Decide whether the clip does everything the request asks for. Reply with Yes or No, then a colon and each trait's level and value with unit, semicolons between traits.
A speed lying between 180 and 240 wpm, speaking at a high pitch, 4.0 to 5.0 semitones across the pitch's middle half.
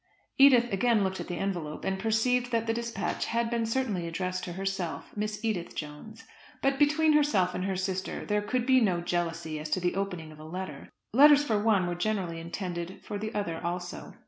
Yes: average, 200 wpm; high, 195 Hz; average, 4.7 semitones